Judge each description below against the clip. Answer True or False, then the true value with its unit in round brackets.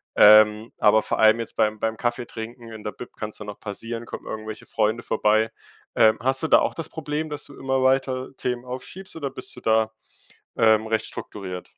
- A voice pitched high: False (115 Hz)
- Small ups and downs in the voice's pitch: False (3.0 semitones)